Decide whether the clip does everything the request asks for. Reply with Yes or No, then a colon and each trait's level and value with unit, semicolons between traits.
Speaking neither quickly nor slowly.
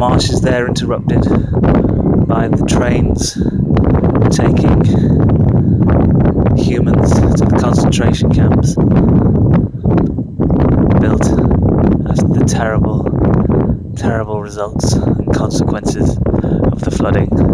No: slow, 80 wpm